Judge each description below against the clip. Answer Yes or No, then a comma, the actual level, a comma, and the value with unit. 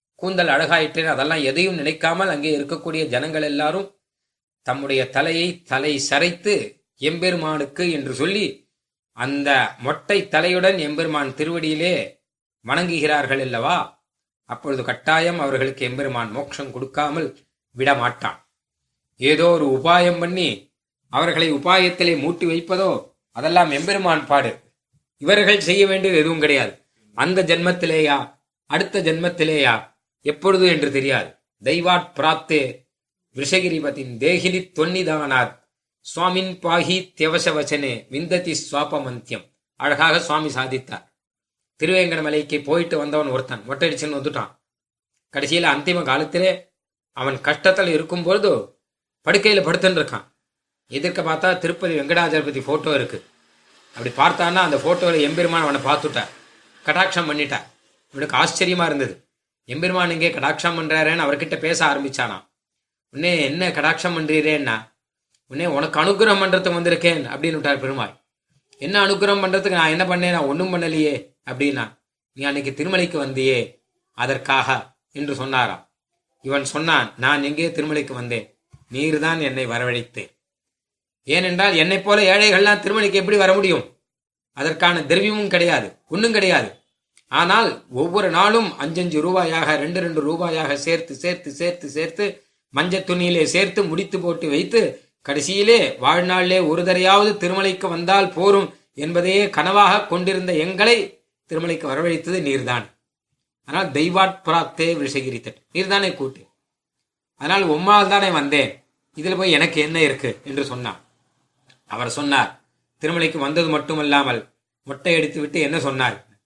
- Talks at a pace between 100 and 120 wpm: Yes, average, 110 wpm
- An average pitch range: Yes, average, 4.1 semitones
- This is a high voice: No, medium, 160 Hz